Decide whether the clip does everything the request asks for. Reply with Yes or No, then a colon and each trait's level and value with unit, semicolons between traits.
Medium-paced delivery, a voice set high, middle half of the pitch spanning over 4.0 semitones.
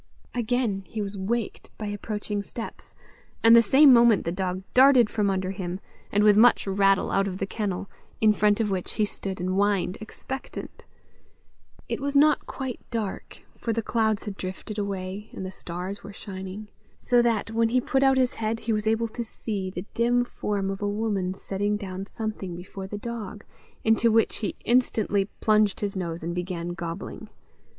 No: average, 185 wpm; high, 205 Hz; average, 2.9 semitones